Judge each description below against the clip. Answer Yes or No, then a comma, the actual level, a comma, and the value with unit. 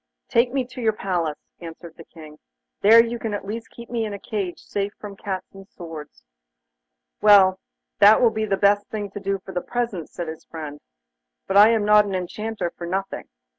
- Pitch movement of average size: Yes, average, 3.5 semitones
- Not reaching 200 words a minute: No, fast, 205 wpm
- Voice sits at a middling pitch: No, high, 200 Hz